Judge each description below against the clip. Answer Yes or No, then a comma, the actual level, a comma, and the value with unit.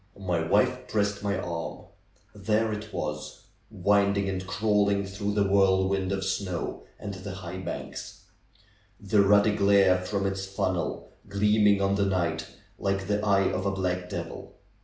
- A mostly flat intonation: Yes, narrow, 1.3 semitones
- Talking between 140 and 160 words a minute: Yes, average, 150 wpm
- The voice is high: No, low, 100 Hz